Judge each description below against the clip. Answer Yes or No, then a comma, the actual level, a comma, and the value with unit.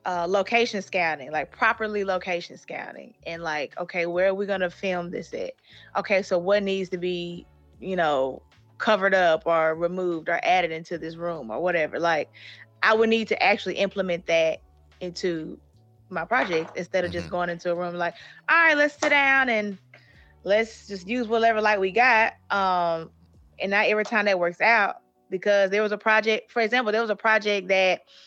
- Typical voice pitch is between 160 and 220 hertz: Yes, medium, 185 Hz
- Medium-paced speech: Yes, average, 185 wpm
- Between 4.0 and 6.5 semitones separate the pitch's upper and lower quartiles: Yes, average, 4.3 semitones